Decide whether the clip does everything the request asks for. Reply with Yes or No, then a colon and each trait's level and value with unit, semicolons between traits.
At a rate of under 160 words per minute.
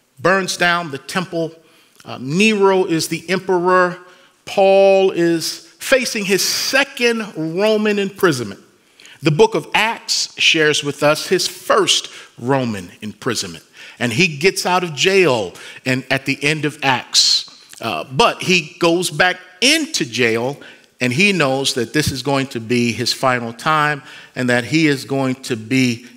Yes: average, 150 wpm